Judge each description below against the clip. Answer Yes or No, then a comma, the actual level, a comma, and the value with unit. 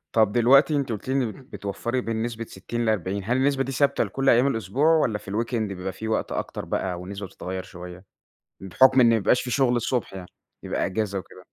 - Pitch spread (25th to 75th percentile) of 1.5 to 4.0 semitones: No, average, 4.8 semitones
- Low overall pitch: Yes, low, 115 Hz